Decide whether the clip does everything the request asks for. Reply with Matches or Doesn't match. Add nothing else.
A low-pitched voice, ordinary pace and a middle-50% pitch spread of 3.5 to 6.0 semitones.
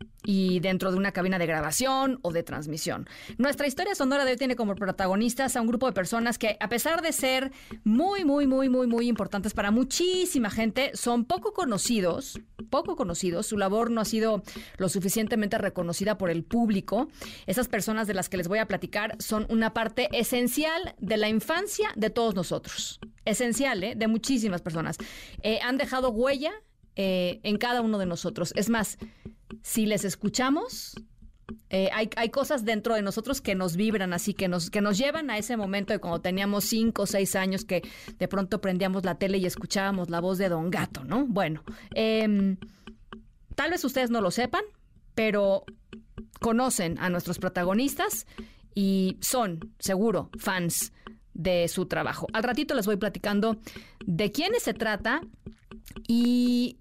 Doesn't match